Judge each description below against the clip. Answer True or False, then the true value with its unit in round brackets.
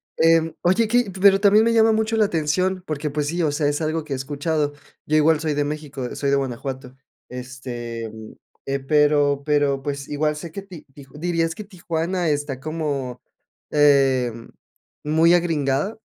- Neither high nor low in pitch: True (150 Hz)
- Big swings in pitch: False (3.4 semitones)